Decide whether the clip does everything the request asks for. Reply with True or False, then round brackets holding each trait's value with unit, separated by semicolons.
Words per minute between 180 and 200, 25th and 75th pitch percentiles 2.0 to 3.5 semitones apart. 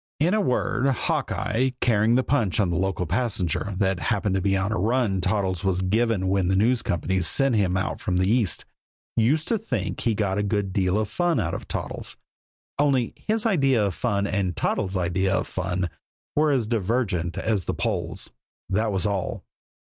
False (185 wpm; 4.3 semitones)